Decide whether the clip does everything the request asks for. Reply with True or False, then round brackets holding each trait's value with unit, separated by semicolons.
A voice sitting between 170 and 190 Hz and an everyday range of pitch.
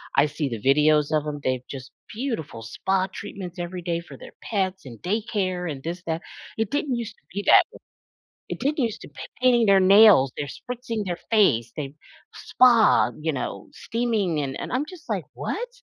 False (185 Hz; 7.0 semitones)